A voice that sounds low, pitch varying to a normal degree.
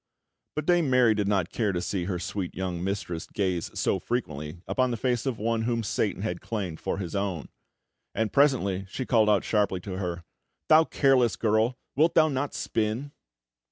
Yes: low, 105 Hz; average, 5.0 semitones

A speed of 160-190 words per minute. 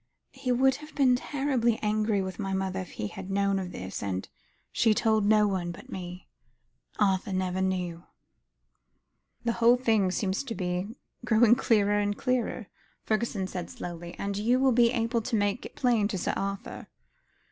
Yes: average, 170 wpm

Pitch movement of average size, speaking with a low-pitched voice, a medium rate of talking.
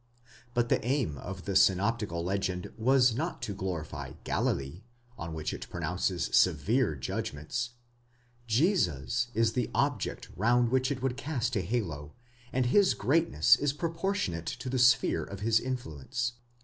No: wide, 6.8 semitones; low, 110 Hz; average, 145 wpm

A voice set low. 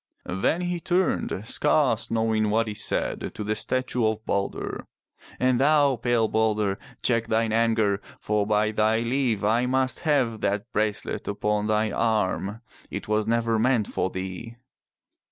Yes: low, 110 Hz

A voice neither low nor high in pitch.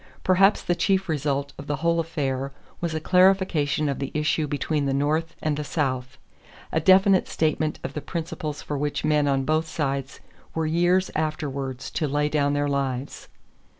Yes: medium, 150 Hz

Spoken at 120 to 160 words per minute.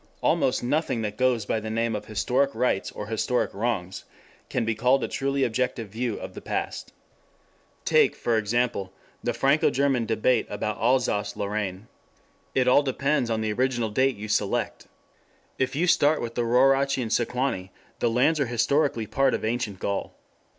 No: average, 170 wpm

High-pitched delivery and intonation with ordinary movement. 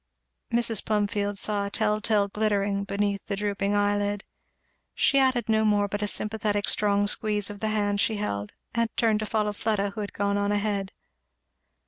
No: high, 205 Hz; narrow, 1.1 semitones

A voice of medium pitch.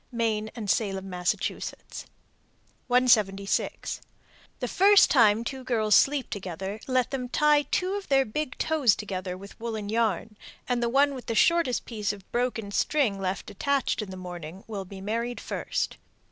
No: high, 225 Hz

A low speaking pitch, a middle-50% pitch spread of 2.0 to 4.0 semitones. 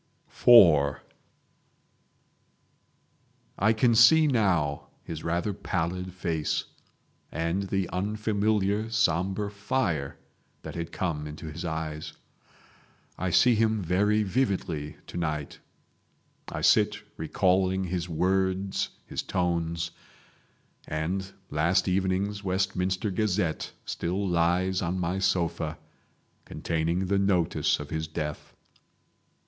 Yes: very low, 90 Hz; average, 3.2 semitones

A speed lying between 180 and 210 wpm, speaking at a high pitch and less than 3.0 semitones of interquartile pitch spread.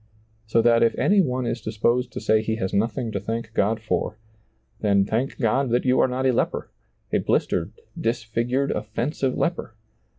No: average, 190 wpm; low, 115 Hz; narrow, 2.6 semitones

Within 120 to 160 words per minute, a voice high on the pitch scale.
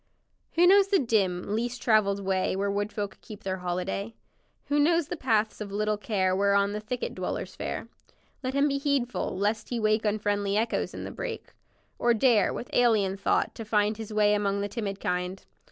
No: average, 190 wpm; high, 210 Hz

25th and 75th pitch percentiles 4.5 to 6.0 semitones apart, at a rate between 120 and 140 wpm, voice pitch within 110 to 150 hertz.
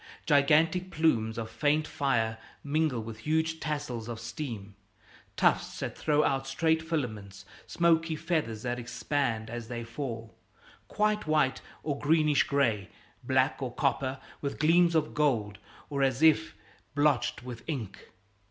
Yes: average, 5.2 semitones; slow, 135 wpm; medium, 140 Hz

